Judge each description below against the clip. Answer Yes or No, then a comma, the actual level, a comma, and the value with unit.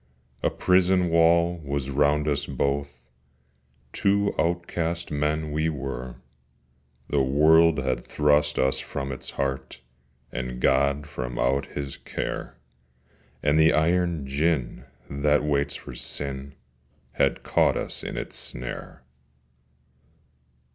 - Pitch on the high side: No, very low, 75 Hz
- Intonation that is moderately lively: Yes, average, 3.0 semitones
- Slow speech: Yes, slow, 115 wpm